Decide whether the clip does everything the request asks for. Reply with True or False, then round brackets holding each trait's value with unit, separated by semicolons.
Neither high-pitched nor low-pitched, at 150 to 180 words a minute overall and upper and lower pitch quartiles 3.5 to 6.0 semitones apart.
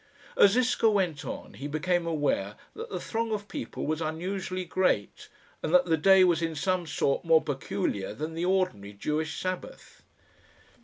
True (170 Hz; 165 wpm; 4.0 semitones)